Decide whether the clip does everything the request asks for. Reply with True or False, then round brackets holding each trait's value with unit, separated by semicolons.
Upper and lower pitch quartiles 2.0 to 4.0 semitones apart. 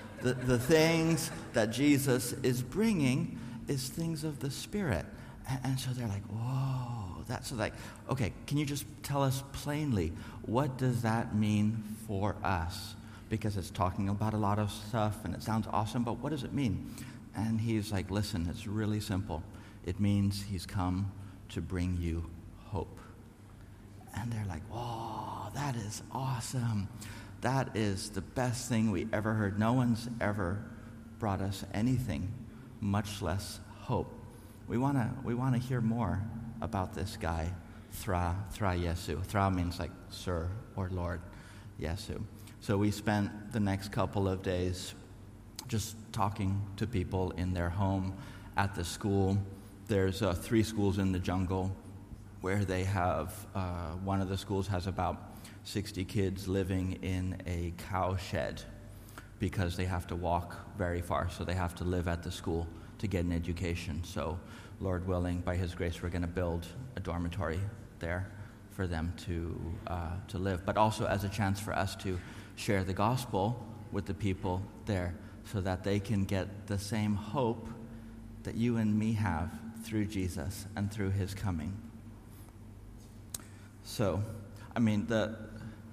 True (3.0 semitones)